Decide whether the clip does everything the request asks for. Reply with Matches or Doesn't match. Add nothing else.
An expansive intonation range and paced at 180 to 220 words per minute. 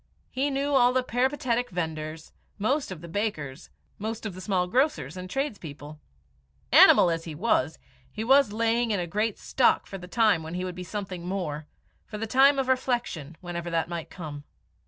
Matches